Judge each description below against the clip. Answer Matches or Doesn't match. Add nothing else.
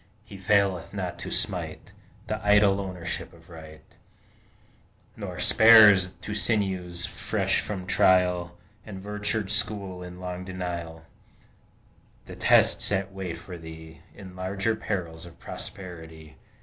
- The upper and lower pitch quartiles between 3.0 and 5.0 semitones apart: Doesn't match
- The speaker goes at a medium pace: Doesn't match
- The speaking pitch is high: Doesn't match